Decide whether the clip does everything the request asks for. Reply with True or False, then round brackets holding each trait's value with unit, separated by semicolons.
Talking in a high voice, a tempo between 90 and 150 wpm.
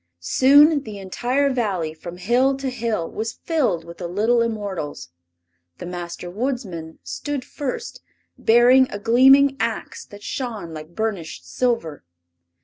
True (225 Hz; 135 wpm)